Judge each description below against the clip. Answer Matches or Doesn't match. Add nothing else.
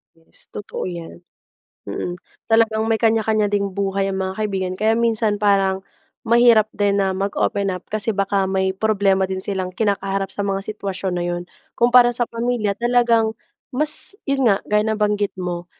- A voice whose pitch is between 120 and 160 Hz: Doesn't match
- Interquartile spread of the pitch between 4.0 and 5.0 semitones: Doesn't match